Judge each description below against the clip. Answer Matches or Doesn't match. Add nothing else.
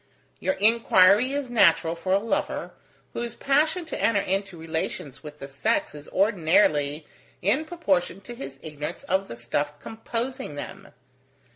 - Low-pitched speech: Doesn't match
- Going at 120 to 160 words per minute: Matches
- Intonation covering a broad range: Matches